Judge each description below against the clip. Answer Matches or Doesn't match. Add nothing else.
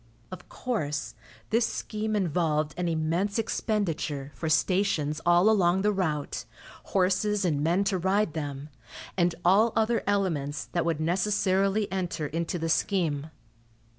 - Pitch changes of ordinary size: Matches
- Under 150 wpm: Matches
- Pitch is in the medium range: Matches